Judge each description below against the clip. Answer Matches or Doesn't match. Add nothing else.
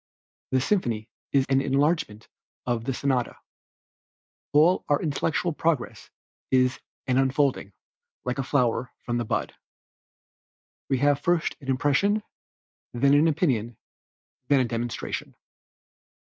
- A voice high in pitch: Doesn't match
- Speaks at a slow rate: Matches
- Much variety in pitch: Doesn't match